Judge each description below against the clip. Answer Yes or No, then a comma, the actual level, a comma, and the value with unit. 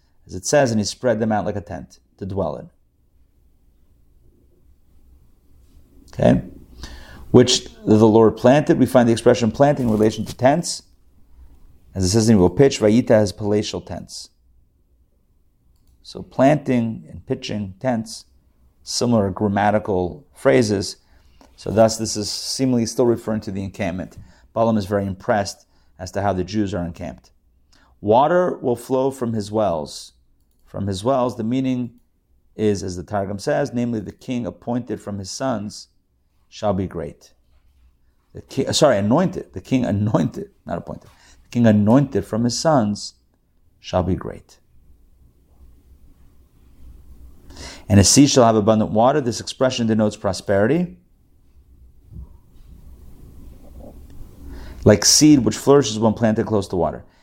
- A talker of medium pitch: No, low, 100 Hz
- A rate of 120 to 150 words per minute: Yes, average, 140 wpm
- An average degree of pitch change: No, wide, 7.8 semitones